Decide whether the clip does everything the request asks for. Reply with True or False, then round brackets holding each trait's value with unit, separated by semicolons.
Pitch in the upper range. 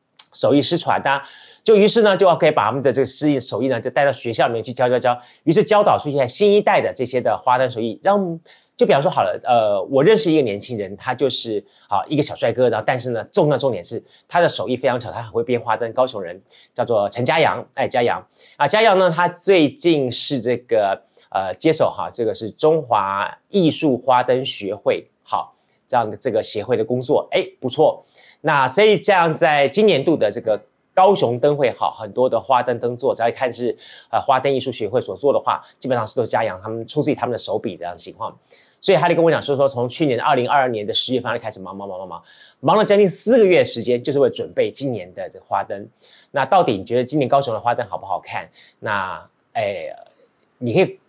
False (140 Hz)